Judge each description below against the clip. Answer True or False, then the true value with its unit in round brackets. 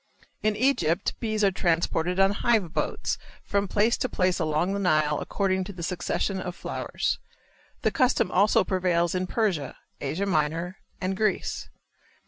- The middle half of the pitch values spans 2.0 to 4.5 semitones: True (2.9 semitones)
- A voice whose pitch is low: False (185 Hz)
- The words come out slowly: False (150 wpm)